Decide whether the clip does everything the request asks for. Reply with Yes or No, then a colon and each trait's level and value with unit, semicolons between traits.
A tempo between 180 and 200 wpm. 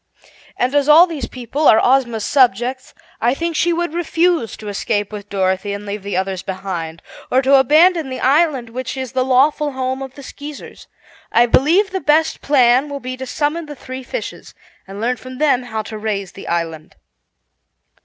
Yes: average, 185 wpm